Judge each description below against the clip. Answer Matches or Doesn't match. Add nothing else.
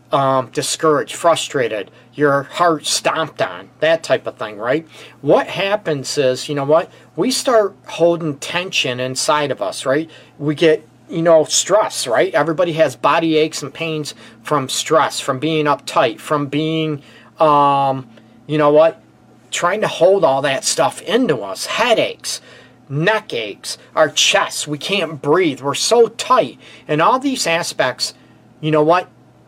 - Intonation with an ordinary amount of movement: Matches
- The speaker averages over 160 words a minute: Doesn't match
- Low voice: Doesn't match